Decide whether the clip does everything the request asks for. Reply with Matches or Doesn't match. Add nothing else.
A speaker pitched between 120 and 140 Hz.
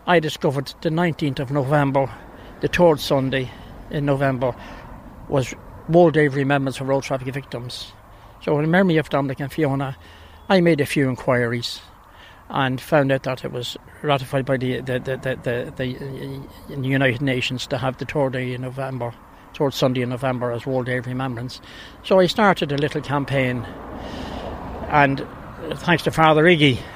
Matches